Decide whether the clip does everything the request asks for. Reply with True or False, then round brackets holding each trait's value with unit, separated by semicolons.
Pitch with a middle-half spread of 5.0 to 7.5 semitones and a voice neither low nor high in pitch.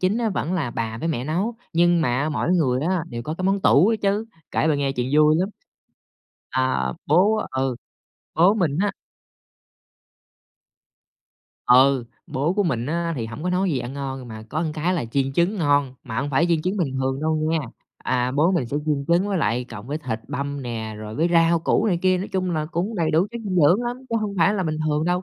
True (5.5 semitones; 155 Hz)